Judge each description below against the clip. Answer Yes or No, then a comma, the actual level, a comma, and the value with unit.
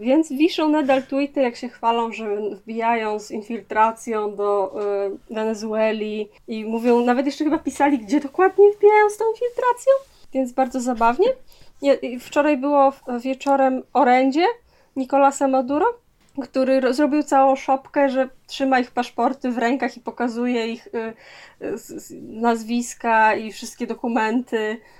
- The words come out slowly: No, average, 140 wpm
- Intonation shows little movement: No, average, 3.8 semitones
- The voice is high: Yes, very high, 255 Hz